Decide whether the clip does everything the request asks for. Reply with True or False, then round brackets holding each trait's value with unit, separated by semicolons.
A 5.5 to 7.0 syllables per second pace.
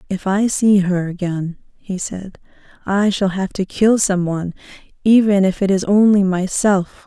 False (4.4 syllables/s)